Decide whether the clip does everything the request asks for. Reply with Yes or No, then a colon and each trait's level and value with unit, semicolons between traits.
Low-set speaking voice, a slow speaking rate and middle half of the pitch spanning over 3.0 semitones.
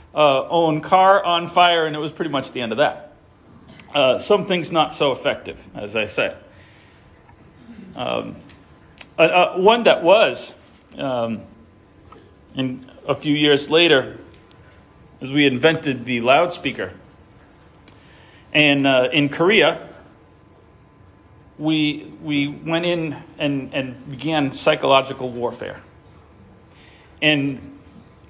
No: medium, 145 Hz; slow, 110 wpm; average, 3.7 semitones